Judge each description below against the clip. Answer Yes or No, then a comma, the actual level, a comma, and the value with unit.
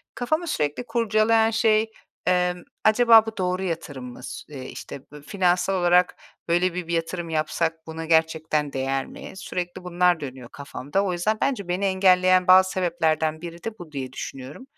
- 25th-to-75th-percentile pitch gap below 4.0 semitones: Yes, average, 3.5 semitones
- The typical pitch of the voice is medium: Yes, medium, 175 Hz